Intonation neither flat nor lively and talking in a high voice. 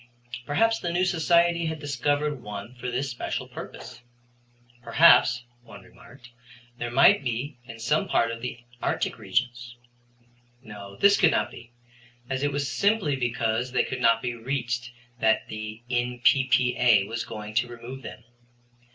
No: average, 3.8 semitones; low, 125 Hz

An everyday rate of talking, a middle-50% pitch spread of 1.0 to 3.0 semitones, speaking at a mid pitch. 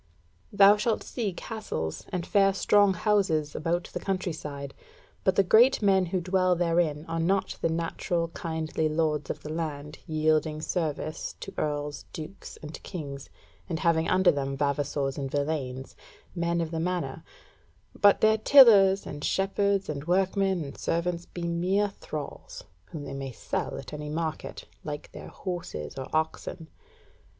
No: average, 155 wpm; average, 4.1 semitones; medium, 165 Hz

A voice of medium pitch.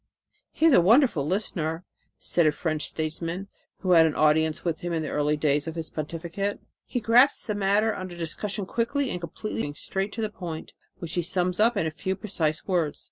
Yes: medium, 175 Hz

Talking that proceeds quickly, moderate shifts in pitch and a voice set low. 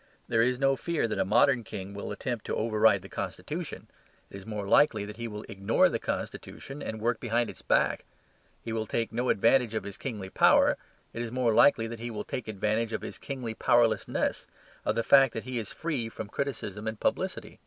No: fast, 210 wpm; narrow, 2.3 semitones; low, 115 Hz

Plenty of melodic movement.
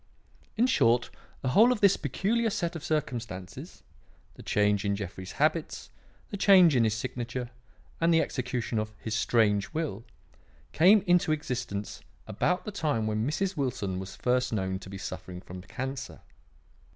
Yes: wide, 8.0 semitones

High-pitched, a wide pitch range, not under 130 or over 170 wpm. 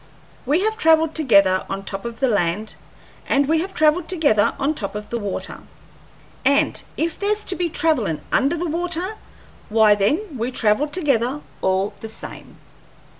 Yes: very high, 280 Hz; wide, 7.6 semitones; average, 165 wpm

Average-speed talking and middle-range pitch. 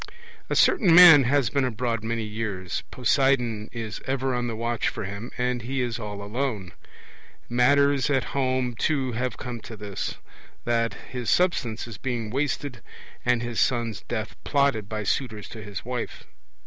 No: average, 160 wpm; low, 120 Hz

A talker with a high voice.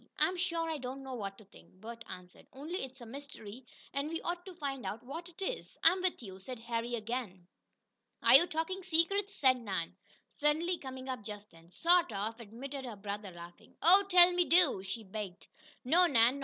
Yes: very high, 260 Hz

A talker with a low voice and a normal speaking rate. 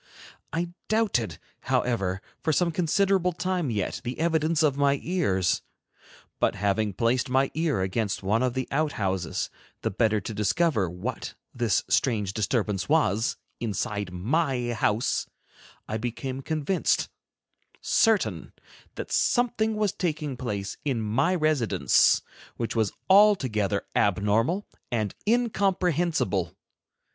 No: low, 125 Hz; slow, 115 wpm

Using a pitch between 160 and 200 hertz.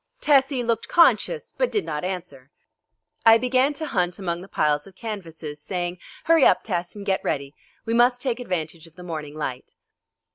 Yes: medium, 185 Hz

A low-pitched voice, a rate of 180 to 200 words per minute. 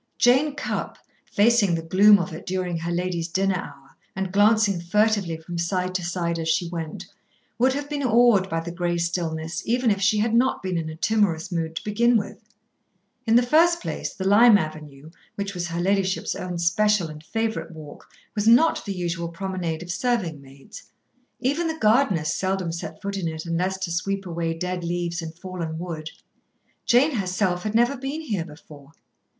No: medium, 185 Hz; average, 185 wpm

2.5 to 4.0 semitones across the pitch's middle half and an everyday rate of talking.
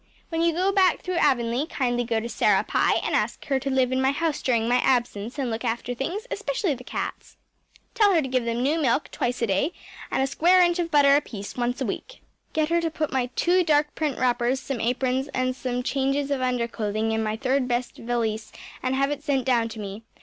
No: average, 3.7 semitones; fast, 230 wpm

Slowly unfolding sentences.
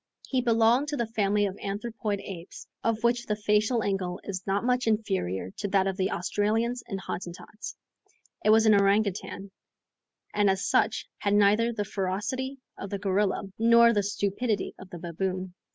No: average, 170 wpm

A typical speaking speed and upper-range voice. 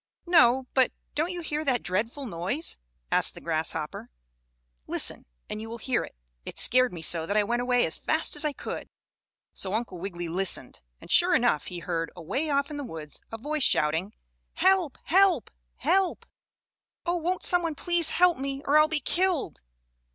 Yes: average, 180 wpm; very high, 260 Hz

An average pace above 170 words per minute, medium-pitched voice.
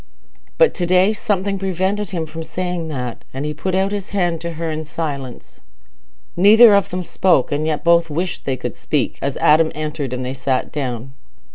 Yes: average, 190 wpm; medium, 165 Hz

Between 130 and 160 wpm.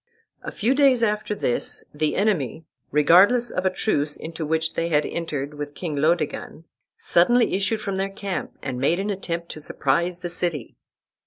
No: average, 170 wpm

